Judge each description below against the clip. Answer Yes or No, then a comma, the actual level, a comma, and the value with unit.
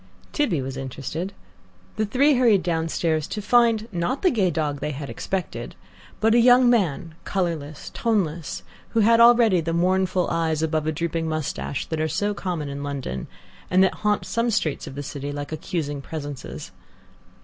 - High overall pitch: No, medium, 170 Hz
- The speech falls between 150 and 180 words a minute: Yes, average, 165 wpm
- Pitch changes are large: Yes, wide, 6.1 semitones